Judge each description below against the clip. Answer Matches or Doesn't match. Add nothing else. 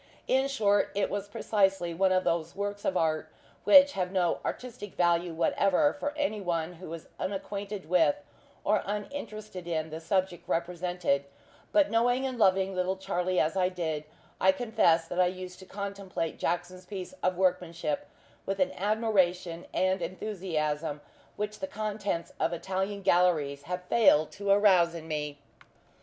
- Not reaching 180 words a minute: Matches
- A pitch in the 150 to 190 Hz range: Matches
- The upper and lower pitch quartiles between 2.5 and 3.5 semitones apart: Matches